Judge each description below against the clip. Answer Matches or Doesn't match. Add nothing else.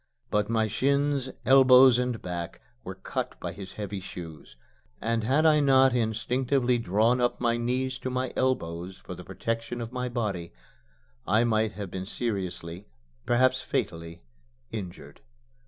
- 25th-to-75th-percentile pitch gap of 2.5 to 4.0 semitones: Doesn't match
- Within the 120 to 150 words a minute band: Matches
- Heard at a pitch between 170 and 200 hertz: Doesn't match